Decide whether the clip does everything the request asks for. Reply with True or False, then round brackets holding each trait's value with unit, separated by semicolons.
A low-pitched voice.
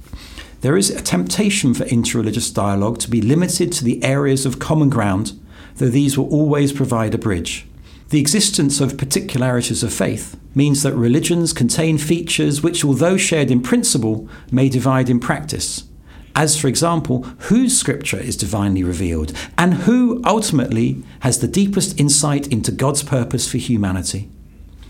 True (130 Hz)